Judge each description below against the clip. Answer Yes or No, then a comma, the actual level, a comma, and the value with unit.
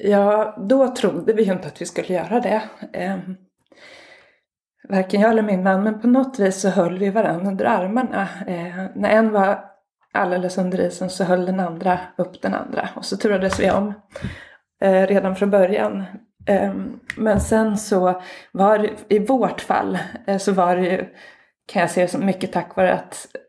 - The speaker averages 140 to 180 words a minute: Yes, average, 170 wpm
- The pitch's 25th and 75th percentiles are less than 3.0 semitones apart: Yes, narrow, 2.5 semitones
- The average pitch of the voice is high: Yes, high, 195 Hz